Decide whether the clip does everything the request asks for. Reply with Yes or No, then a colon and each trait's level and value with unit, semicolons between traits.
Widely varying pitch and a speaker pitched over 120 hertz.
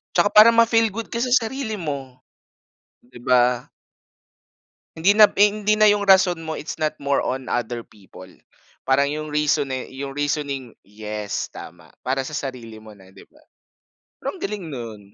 Yes: wide, 8.8 semitones; medium, 140 Hz